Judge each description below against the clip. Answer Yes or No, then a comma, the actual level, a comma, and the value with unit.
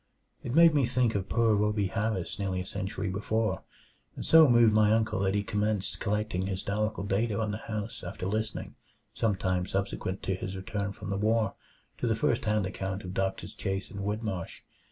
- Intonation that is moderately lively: No, narrow, 2.3 semitones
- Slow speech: No, average, 190 wpm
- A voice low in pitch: Yes, low, 105 Hz